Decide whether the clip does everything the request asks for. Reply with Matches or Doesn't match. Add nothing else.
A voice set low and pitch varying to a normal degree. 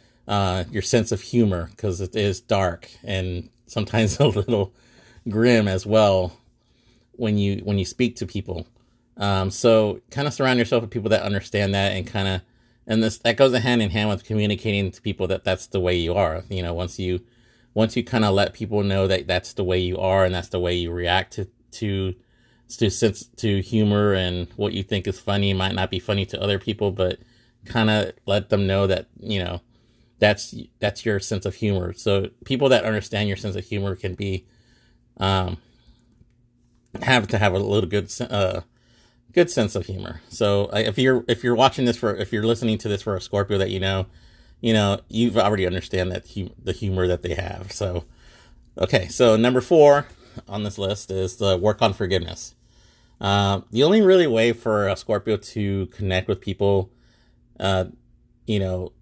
Matches